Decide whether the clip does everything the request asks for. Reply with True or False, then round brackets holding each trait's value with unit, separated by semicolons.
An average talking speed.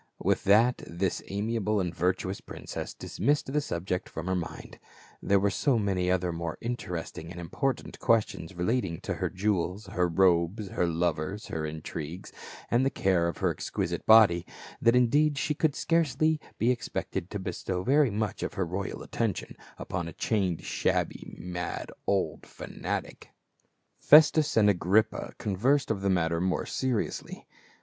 True (155 wpm)